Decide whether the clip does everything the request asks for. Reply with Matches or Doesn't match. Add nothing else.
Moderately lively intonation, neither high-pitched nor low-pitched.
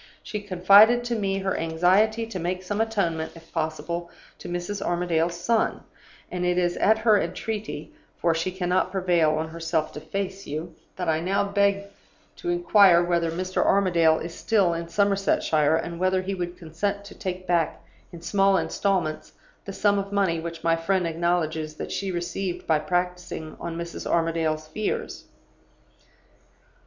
Matches